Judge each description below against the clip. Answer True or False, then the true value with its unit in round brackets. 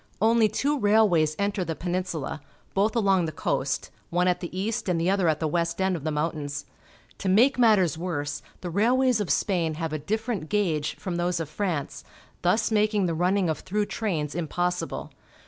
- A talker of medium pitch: True (180 Hz)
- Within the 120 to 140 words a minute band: False (185 wpm)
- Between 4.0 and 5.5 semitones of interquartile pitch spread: True (4.4 semitones)